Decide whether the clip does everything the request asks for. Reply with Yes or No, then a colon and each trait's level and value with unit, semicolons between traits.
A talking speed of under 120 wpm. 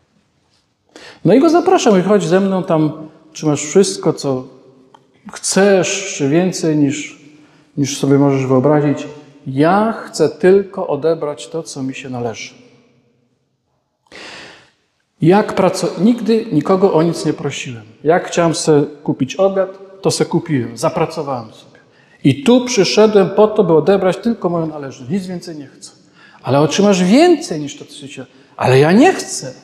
No: average, 150 wpm